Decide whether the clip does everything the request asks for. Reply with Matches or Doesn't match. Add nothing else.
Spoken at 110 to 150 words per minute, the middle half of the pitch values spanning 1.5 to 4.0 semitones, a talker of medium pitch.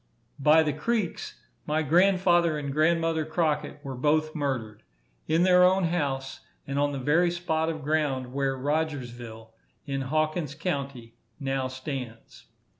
Matches